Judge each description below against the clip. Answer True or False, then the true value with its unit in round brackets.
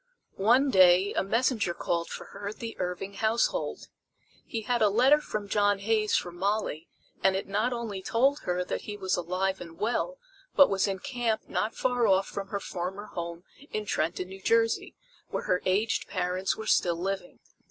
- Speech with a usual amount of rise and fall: True (3.5 semitones)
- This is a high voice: True (200 Hz)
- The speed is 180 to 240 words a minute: True (185 wpm)